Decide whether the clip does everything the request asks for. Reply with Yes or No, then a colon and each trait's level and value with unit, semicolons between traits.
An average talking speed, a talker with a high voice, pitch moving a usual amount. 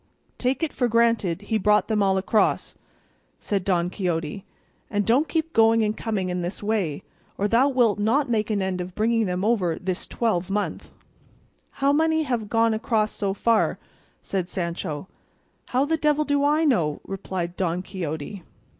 Yes: average, 165 wpm; high, 210 Hz; average, 4.3 semitones